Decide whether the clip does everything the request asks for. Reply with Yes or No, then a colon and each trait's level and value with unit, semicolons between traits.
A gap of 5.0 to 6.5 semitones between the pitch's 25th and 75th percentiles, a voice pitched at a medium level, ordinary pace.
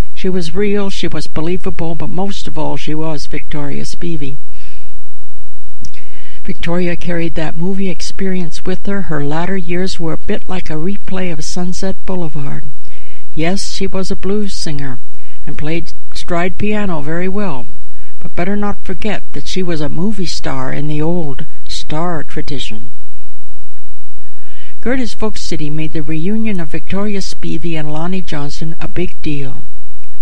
Yes: average, 5.3 semitones; medium, 165 Hz; average, 150 wpm